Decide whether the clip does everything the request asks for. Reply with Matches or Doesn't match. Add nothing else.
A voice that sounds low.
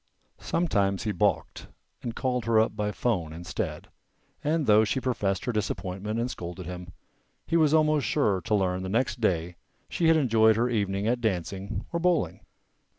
Matches